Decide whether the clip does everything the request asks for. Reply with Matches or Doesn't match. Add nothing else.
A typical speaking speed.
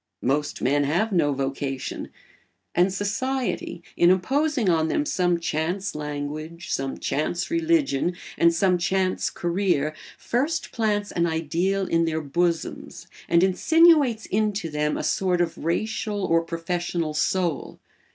Doesn't match